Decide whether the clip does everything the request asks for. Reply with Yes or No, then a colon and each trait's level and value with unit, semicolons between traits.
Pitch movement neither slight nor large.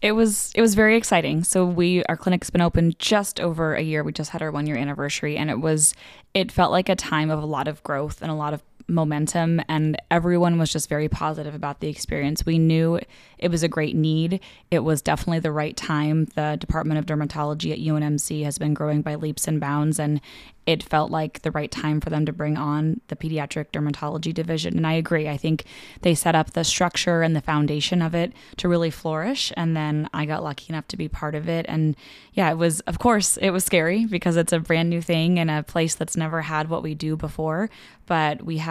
No: narrow, 1.9 semitones